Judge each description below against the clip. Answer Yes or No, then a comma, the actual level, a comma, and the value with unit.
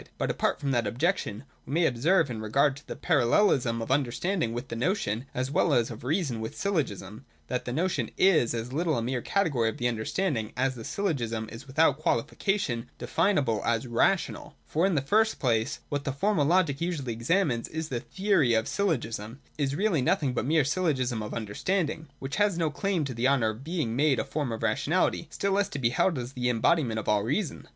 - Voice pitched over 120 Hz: Yes, low, 135 Hz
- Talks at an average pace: No, fast, 210 wpm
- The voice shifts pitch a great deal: Yes, wide, 6.0 semitones